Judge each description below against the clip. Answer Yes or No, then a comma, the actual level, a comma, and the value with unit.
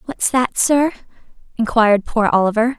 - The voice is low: No, high, 235 Hz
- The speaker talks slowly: Yes, slow, 130 wpm